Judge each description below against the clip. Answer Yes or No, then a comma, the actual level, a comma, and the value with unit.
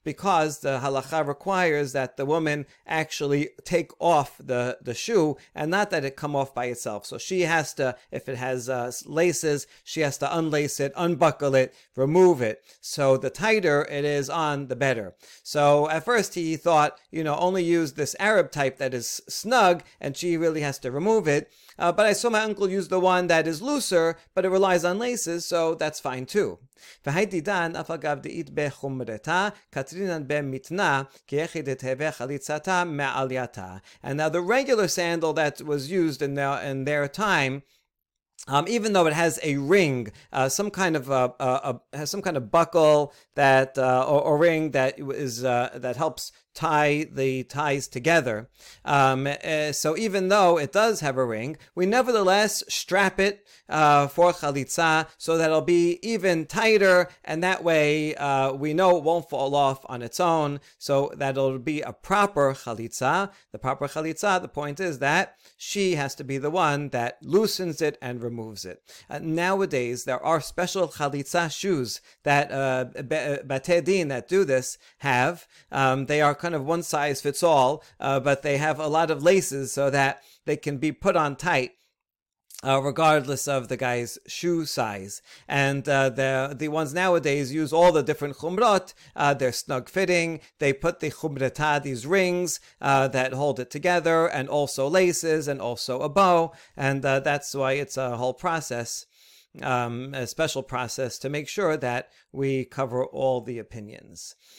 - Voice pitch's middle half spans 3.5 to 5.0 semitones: Yes, average, 4.0 semitones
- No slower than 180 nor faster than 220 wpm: No, average, 170 wpm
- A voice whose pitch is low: No, medium, 145 Hz